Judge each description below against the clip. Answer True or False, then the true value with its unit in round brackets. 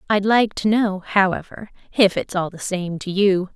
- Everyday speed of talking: True (185 wpm)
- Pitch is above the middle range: True (195 Hz)